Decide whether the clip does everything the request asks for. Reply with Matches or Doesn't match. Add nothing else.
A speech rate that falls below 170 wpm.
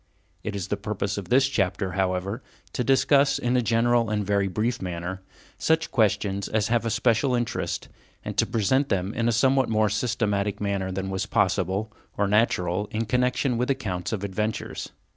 Doesn't match